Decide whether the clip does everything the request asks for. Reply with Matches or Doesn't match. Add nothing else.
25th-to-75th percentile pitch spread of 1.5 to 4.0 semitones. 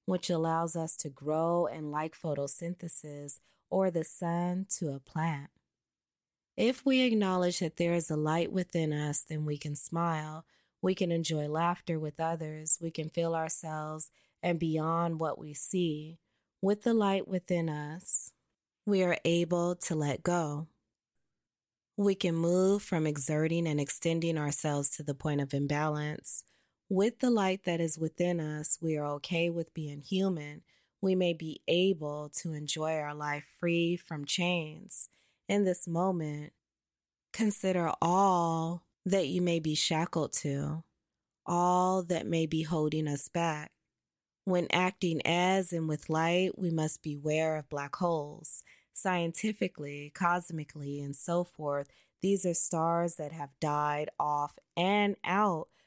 Matches